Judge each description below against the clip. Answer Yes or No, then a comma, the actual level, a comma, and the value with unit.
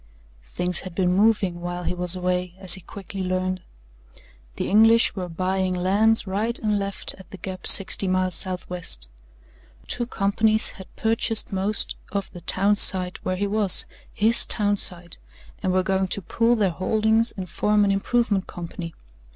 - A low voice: No, high, 190 Hz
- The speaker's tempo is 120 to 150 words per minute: No, average, 165 wpm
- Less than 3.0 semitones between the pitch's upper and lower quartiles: Yes, narrow, 2.4 semitones